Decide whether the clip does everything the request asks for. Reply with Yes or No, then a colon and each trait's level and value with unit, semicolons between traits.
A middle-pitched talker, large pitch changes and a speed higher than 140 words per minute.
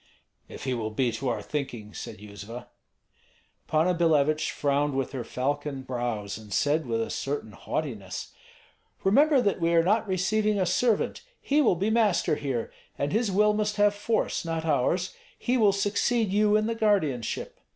Yes: medium, 160 Hz; wide, 8.5 semitones; average, 170 wpm